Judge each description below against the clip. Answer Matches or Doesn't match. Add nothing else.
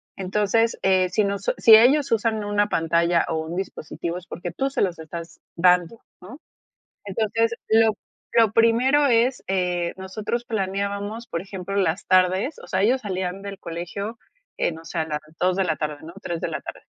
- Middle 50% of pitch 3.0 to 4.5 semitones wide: Matches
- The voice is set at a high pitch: Matches